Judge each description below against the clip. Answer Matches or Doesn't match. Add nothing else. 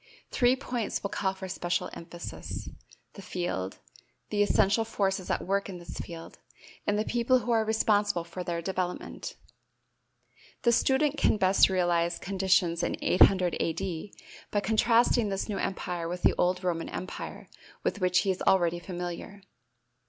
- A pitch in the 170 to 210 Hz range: Matches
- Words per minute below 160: Matches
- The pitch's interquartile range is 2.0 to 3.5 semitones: Matches